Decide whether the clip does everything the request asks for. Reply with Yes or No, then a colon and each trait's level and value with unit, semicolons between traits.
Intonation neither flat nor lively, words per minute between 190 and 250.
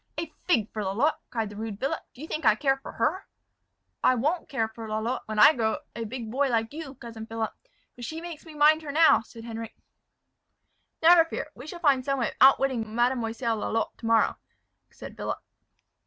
Yes: average, 5.0 semitones; fast, 205 wpm